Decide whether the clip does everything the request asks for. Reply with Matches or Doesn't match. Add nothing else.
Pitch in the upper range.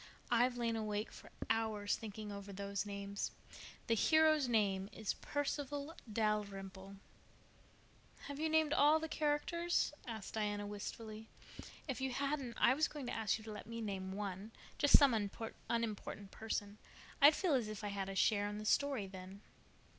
Matches